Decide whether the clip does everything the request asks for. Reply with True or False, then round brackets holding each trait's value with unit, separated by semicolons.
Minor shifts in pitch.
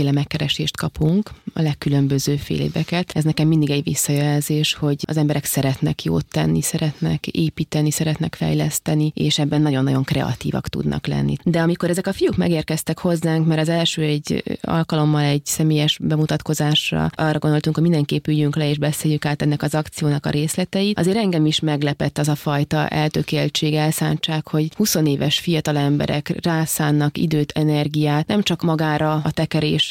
True (1.5 semitones)